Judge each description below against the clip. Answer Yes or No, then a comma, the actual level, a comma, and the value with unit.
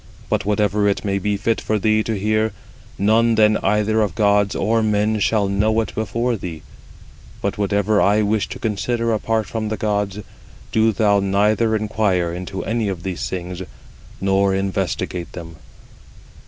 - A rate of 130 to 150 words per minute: No, average, 160 wpm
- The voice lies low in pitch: Yes, low, 105 Hz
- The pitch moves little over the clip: Yes, narrow, 1.9 semitones